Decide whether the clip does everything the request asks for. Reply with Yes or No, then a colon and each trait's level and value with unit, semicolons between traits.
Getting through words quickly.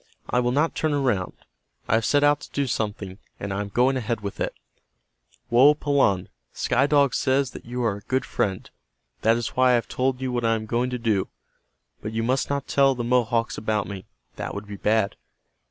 Yes: fast, 210 wpm